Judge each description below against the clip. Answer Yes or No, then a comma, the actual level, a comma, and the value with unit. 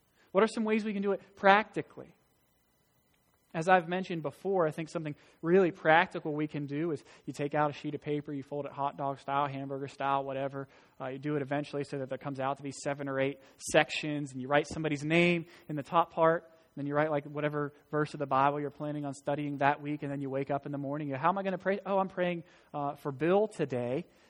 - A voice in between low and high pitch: Yes, medium, 150 Hz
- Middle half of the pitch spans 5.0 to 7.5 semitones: No, average, 2.8 semitones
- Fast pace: Yes, fast, 250 wpm